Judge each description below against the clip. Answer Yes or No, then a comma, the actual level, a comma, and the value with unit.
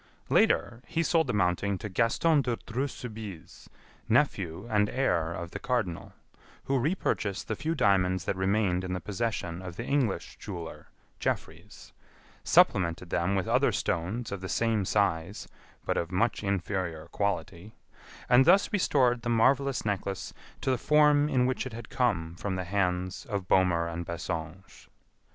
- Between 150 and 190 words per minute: Yes, average, 160 wpm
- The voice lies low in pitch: Yes, low, 100 Hz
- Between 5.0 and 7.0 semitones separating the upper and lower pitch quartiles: Yes, average, 5.3 semitones